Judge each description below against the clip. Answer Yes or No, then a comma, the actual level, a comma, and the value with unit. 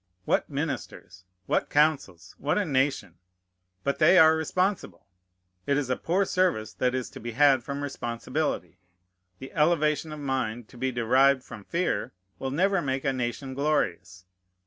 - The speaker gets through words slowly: No, average, 155 wpm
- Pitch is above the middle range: No, low, 135 Hz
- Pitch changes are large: No, average, 4.5 semitones